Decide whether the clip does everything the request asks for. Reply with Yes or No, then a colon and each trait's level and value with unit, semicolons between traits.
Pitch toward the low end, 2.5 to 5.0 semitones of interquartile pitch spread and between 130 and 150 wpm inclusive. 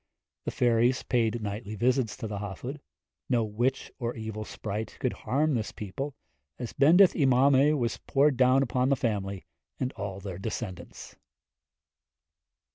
Yes: low, 120 Hz; average, 4.0 semitones; average, 145 wpm